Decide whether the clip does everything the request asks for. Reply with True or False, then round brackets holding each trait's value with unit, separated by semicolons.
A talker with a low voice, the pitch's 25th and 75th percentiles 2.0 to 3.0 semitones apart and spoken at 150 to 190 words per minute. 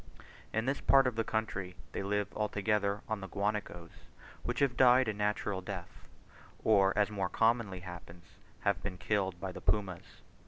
True (105 Hz; 2.6 semitones; 165 wpm)